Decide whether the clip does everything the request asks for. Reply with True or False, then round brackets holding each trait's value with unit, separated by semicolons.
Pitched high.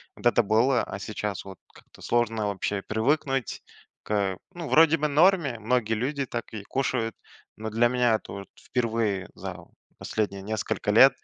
False (115 Hz)